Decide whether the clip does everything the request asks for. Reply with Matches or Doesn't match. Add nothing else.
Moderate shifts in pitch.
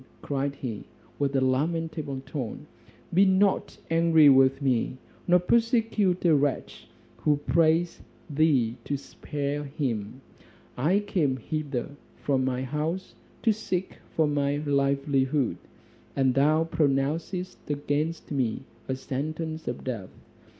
Matches